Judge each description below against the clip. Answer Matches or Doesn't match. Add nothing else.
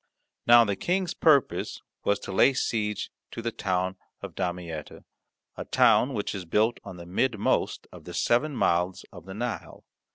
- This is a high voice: Doesn't match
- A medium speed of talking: Matches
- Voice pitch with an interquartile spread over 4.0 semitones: Matches